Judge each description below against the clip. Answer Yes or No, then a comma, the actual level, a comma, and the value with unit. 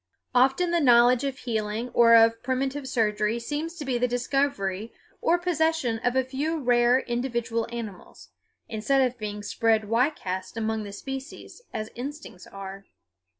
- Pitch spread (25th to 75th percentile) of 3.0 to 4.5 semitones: Yes, average, 3.5 semitones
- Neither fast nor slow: Yes, average, 150 wpm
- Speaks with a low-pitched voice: No, high, 240 Hz